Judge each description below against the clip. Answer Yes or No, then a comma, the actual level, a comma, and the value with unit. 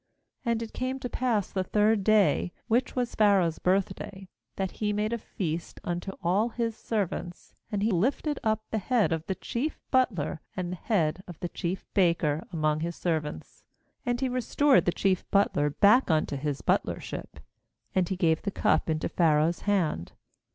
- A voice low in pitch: No, high, 190 Hz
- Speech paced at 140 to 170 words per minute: No, average, 180 wpm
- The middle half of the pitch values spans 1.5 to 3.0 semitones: No, average, 4.7 semitones